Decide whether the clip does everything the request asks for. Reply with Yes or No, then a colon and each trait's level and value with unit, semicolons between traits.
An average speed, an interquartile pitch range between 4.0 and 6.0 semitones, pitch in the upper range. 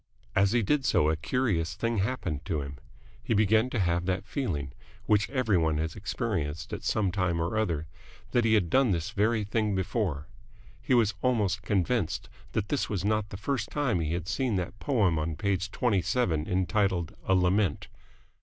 No: average, 185 wpm; average, 4.6 semitones; low, 100 Hz